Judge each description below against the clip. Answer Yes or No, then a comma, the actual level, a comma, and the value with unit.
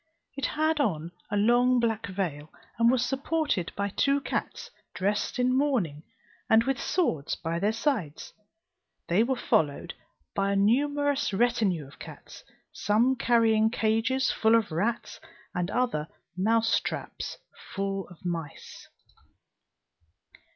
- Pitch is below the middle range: No, high, 220 Hz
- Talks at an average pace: No, slow, 125 wpm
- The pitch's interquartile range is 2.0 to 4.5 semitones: No, wide, 5.4 semitones